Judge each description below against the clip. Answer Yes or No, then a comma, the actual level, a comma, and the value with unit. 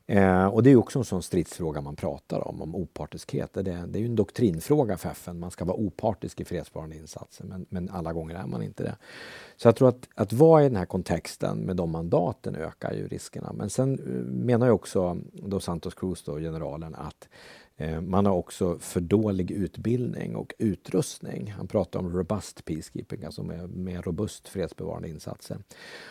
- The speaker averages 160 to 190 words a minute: Yes, average, 185 wpm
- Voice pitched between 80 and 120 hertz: Yes, very low, 90 Hz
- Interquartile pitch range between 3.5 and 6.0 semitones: Yes, average, 4.0 semitones